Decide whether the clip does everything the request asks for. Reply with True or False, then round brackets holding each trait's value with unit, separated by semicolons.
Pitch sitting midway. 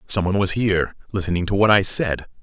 False (95 Hz)